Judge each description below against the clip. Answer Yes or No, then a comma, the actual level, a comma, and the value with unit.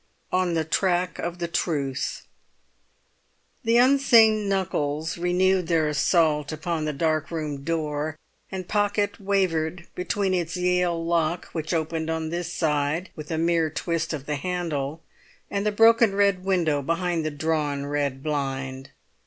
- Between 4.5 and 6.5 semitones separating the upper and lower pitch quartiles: No, average, 3.2 semitones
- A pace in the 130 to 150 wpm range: Yes, average, 145 wpm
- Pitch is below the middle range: No, medium, 165 Hz